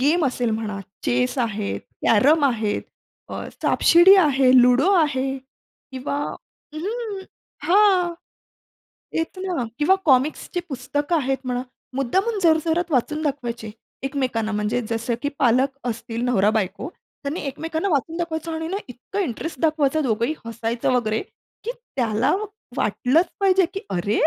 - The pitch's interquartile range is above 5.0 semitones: Yes, wide, 5.6 semitones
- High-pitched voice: Yes, very high, 270 Hz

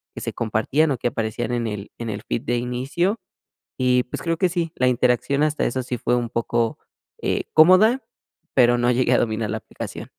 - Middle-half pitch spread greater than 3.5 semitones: Yes, average, 4.4 semitones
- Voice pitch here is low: Yes, low, 125 Hz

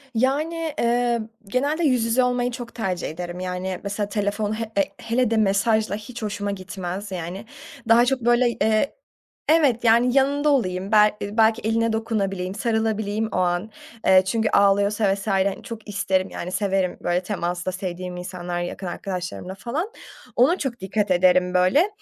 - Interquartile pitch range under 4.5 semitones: Yes, average, 4.0 semitones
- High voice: Yes, high, 210 Hz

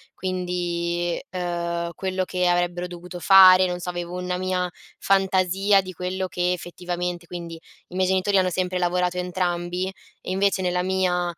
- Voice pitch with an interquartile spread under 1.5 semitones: Yes, narrow, 1.0 semitones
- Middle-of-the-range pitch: Yes, medium, 180 Hz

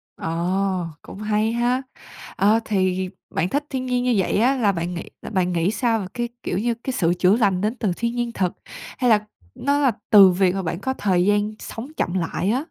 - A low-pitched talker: No, high, 205 Hz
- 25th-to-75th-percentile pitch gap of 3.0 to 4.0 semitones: No, average, 4.5 semitones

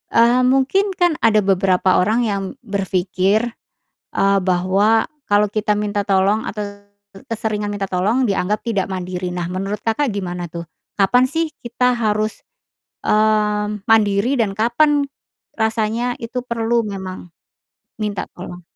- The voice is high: Yes, high, 210 Hz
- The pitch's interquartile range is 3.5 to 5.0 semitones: No, average, 3.0 semitones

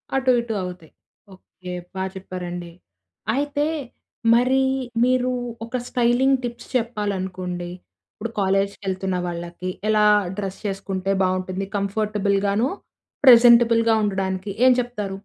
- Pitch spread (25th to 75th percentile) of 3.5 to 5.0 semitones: Yes, average, 4.1 semitones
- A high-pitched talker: Yes, high, 200 Hz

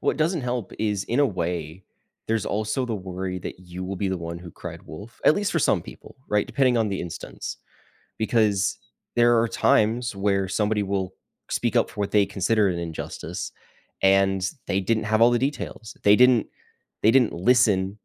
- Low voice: Yes, low, 105 Hz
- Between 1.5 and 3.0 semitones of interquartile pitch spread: No, average, 3.7 semitones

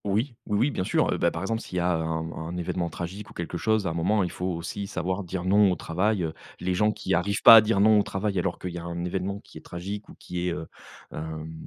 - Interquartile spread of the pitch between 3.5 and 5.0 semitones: No, average, 2.9 semitones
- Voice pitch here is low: Yes, very low, 90 Hz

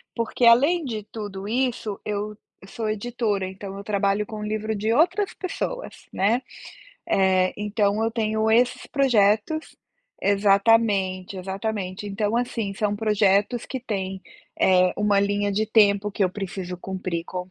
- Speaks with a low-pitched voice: No, high, 210 Hz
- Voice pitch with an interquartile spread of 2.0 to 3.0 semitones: Yes, narrow, 2.4 semitones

